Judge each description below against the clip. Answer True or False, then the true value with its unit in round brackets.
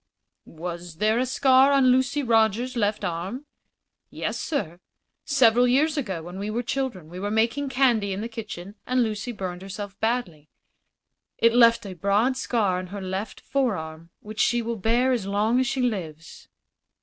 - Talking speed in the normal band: True (170 wpm)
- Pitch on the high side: True (220 Hz)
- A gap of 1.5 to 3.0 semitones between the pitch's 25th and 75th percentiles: False (4.8 semitones)